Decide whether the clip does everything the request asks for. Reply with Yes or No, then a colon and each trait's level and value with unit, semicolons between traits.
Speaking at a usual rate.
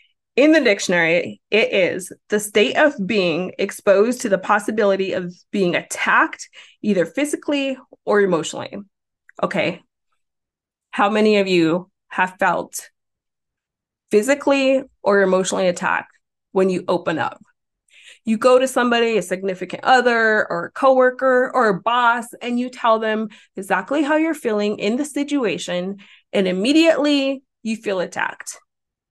No: slow, 130 wpm